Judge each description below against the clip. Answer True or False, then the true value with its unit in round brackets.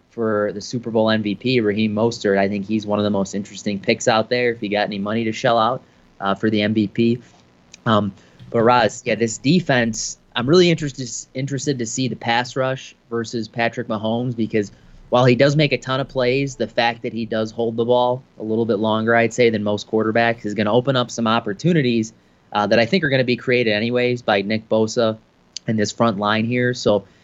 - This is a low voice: True (115 Hz)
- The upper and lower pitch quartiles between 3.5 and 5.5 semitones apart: False (2.8 semitones)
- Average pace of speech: False (220 wpm)